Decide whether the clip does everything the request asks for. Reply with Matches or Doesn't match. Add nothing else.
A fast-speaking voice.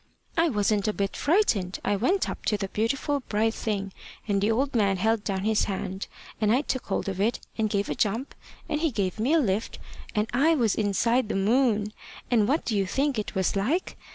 Matches